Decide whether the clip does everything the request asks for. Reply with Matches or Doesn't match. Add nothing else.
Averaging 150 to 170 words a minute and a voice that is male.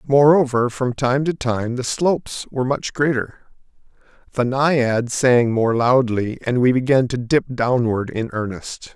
Matches